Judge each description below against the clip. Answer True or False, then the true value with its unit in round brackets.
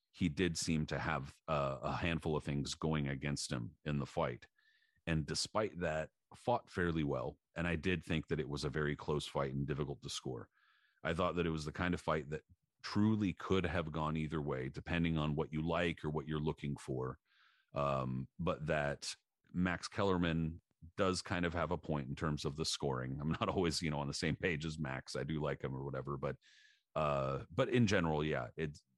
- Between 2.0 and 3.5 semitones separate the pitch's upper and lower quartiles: True (3.2 semitones)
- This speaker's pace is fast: True (215 wpm)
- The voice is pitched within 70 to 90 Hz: True (80 Hz)